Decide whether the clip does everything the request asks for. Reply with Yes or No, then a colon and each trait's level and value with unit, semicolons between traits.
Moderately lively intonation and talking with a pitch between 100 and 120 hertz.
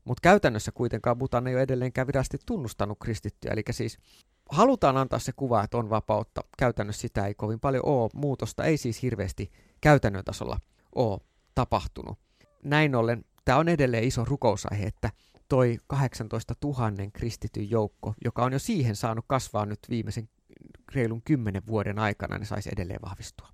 Yes: average, 3.6 semitones; low, 115 Hz